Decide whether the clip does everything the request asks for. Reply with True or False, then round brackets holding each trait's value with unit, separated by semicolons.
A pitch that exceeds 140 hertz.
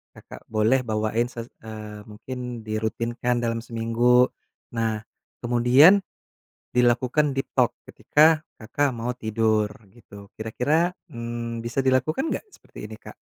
False (120 Hz)